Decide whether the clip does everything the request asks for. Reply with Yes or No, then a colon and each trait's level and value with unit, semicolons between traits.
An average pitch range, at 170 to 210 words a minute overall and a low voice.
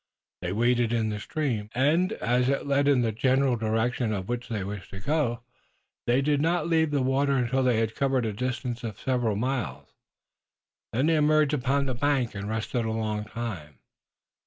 Yes: average, 3.9 semitones; average, 185 wpm; low, 125 Hz